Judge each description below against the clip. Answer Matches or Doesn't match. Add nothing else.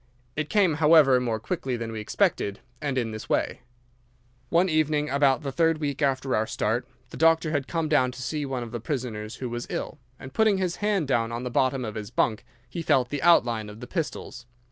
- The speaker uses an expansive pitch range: Doesn't match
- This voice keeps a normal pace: Doesn't match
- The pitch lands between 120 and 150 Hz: Matches